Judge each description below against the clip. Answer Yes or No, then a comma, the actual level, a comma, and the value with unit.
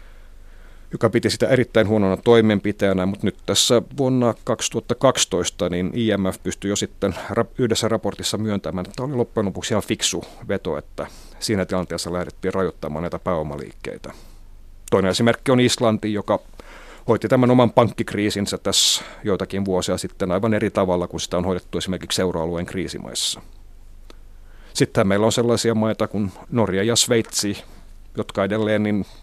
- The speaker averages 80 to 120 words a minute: No, average, 140 wpm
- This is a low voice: Yes, low, 100 Hz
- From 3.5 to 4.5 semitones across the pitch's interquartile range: Yes, average, 3.8 semitones